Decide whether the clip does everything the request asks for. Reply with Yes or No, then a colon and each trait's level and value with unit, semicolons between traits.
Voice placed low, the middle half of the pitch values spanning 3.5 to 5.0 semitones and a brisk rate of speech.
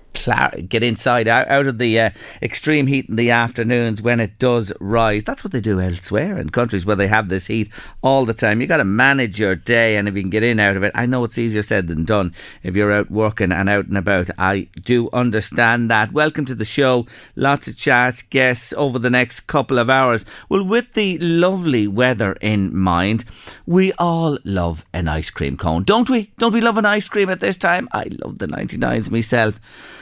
Yes: low, 115 Hz; average, 4.4 semitones; fast, 215 wpm